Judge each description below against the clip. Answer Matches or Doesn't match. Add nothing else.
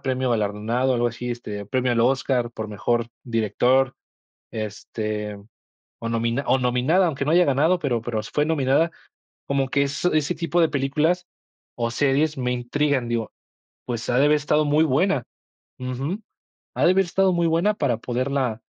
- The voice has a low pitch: Matches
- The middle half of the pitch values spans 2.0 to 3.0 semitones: Doesn't match